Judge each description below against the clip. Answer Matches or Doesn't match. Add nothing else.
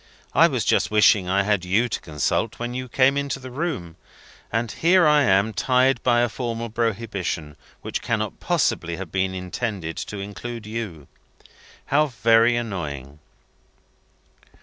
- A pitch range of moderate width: Matches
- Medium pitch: Doesn't match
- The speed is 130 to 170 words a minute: Matches